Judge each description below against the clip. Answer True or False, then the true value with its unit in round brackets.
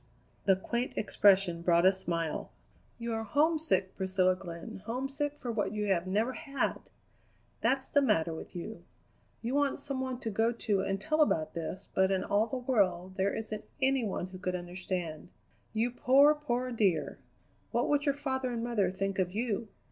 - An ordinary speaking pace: True (180 wpm)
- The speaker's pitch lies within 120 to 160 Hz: False (215 Hz)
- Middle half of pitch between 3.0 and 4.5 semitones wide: False (5.6 semitones)